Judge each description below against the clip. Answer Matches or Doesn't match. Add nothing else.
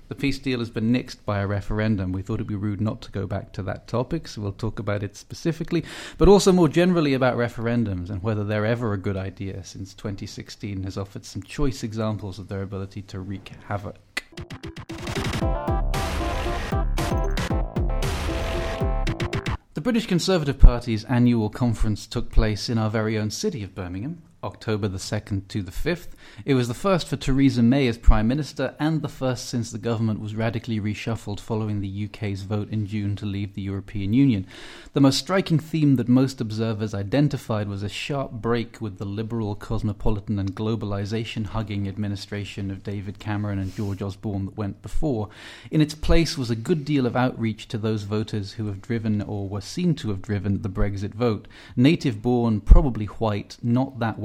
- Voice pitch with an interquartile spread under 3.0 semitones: Doesn't match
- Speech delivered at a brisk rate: Doesn't match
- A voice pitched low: Matches